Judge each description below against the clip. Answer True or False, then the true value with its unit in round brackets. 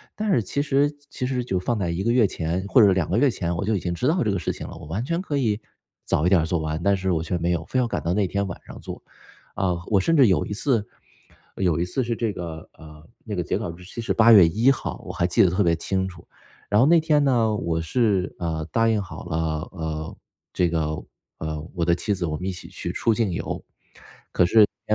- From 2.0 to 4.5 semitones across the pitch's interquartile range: False (5.3 semitones)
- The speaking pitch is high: False (95 Hz)